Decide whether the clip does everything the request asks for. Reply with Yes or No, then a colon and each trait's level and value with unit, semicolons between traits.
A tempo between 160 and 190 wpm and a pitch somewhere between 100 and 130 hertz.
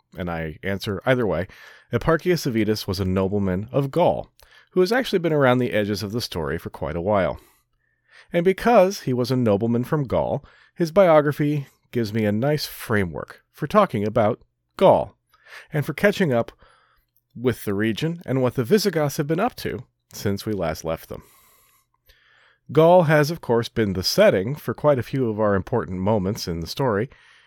Yes: average, 180 wpm; low, 125 Hz